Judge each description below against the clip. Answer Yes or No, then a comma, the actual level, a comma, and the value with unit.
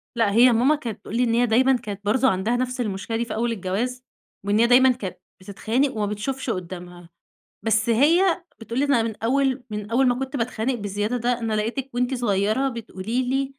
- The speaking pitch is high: Yes, high, 235 Hz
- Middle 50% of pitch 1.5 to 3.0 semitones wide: No, average, 3.4 semitones